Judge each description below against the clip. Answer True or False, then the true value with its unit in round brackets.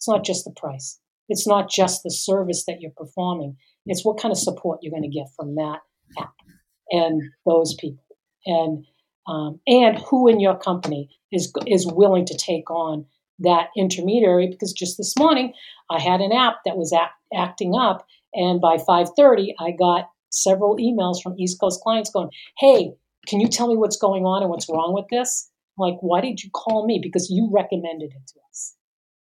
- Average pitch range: True (3.8 semitones)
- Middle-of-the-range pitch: True (180 Hz)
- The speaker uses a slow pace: False (190 wpm)